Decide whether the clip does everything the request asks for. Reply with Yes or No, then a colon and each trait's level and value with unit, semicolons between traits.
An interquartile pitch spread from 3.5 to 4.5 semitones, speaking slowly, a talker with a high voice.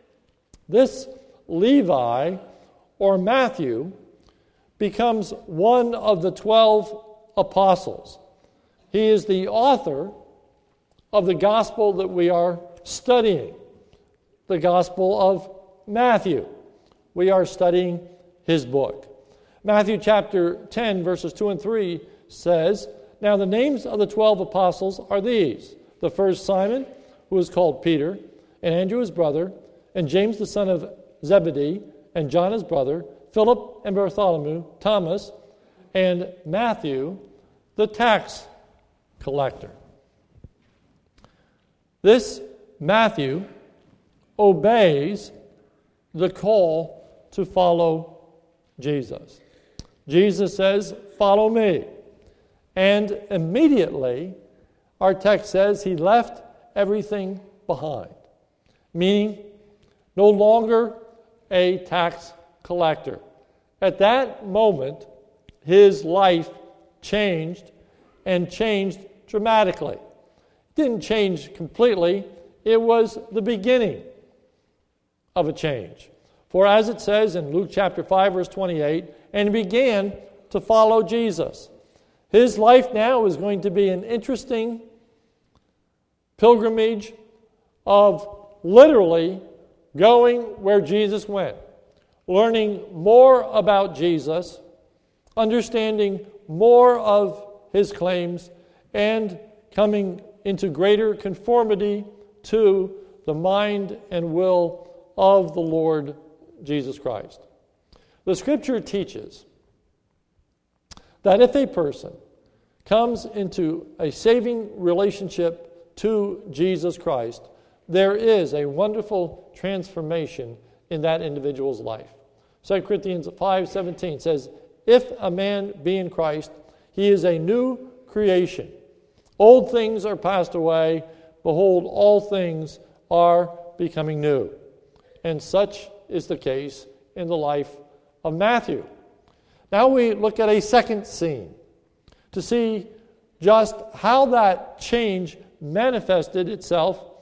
Yes: average, 3.9 semitones; slow, 105 wpm; high, 195 Hz